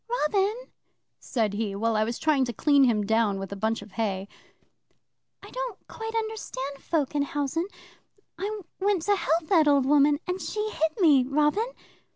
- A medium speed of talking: Yes, average, 175 wpm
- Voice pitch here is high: Yes, very high, 290 Hz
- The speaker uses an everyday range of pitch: No, wide, 8.9 semitones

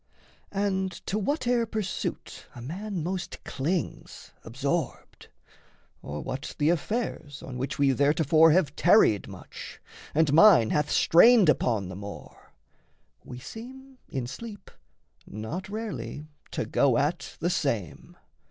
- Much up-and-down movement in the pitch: Yes, wide, 7.2 semitones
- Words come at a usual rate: No, slow, 125 wpm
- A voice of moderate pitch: Yes, medium, 160 Hz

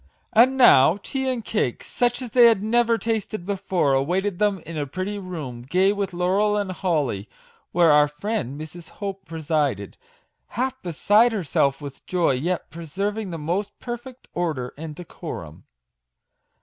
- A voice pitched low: No, medium, 185 Hz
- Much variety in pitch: Yes, wide, 5.7 semitones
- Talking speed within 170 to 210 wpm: No, average, 150 wpm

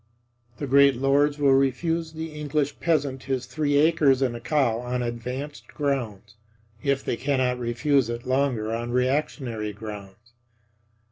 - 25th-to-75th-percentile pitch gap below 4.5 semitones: Yes, average, 3.4 semitones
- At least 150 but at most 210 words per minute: No, average, 140 wpm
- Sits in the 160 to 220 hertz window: No, low, 135 Hz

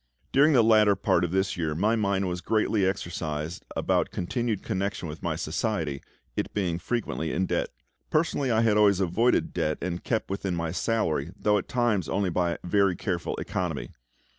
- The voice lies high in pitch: No, very low, 95 Hz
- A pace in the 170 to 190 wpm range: Yes, average, 175 wpm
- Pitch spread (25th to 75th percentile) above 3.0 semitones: Yes, average, 4.1 semitones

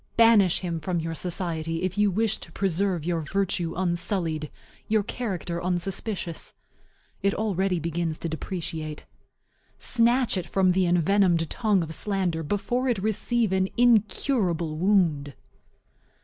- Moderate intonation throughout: Yes, average, 3.5 semitones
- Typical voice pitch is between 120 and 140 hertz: No, medium, 185 Hz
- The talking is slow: Yes, slow, 130 wpm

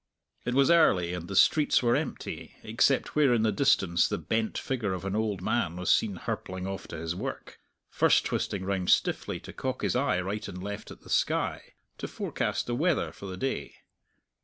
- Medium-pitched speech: No, low, 100 Hz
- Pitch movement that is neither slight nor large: Yes, average, 4.6 semitones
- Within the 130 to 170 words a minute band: No, average, 200 wpm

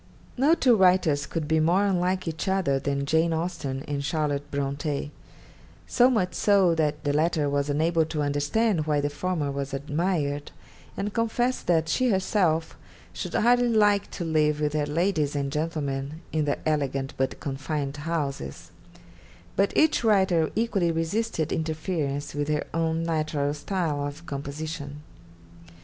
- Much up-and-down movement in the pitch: No, average, 4.0 semitones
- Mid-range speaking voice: Yes, medium, 155 Hz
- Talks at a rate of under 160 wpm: Yes, average, 150 wpm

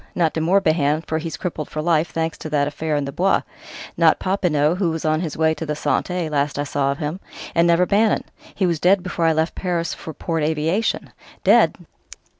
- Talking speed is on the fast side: Yes, fast, 215 wpm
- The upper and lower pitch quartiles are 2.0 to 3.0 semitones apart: Yes, narrow, 2.5 semitones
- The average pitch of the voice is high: No, medium, 160 Hz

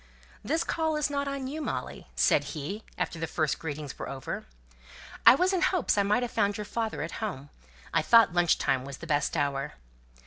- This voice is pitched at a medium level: No, high, 200 Hz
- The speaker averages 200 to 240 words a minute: Yes, fast, 205 wpm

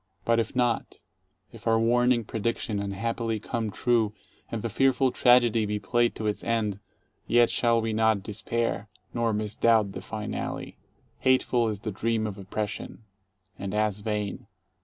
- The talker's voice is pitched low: Yes, low, 110 Hz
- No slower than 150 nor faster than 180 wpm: Yes, average, 155 wpm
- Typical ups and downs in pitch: No, narrow, 1.9 semitones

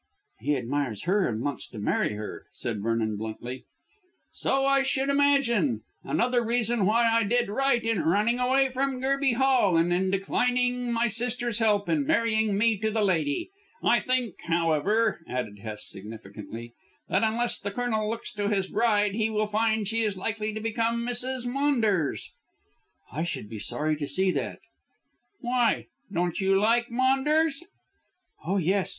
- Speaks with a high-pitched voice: Yes, high, 215 Hz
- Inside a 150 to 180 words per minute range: Yes, average, 160 wpm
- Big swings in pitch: Yes, wide, 6.1 semitones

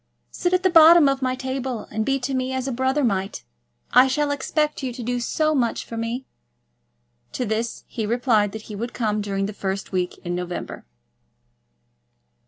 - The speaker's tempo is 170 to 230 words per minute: Yes, average, 190 wpm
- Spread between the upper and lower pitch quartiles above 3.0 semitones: Yes, average, 4.0 semitones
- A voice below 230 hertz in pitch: No, high, 245 Hz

